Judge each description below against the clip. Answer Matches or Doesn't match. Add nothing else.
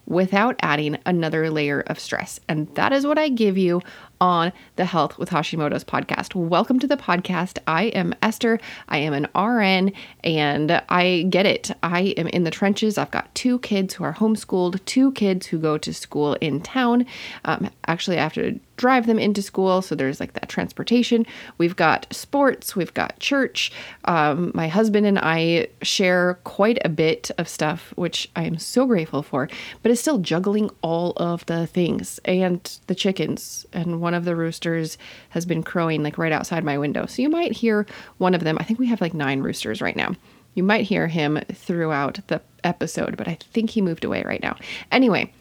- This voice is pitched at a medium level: Matches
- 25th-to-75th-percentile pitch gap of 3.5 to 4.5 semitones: Doesn't match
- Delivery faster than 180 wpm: Matches